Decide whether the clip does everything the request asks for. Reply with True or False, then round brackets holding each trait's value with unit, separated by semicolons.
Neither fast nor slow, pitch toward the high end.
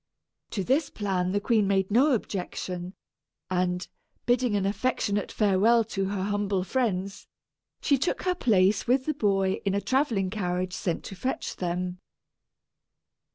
True (145 wpm; 200 Hz)